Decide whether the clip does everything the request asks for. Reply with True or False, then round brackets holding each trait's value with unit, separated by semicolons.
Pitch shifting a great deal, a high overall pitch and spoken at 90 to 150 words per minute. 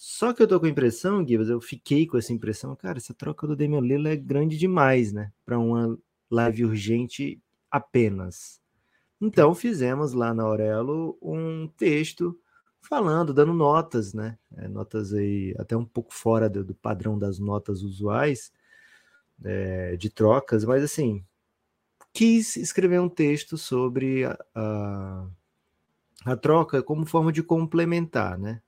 False (6.7 semitones; 120 Hz; 140 wpm)